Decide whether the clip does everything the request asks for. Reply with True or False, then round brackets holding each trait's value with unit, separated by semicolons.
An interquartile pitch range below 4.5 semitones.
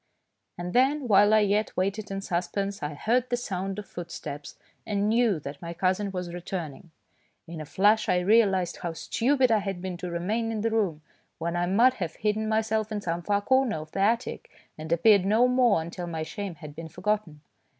True (4.1 semitones)